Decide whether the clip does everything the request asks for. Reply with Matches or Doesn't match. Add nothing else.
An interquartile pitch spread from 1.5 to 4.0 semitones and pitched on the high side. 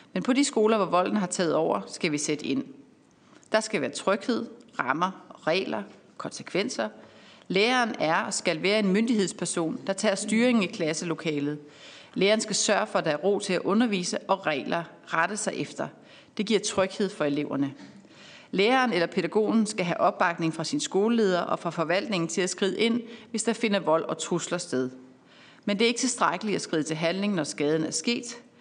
Doesn't match